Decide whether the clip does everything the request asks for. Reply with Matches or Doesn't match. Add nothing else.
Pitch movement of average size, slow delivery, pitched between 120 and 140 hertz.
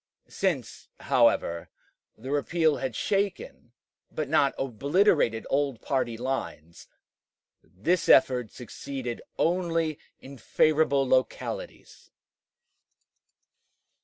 Matches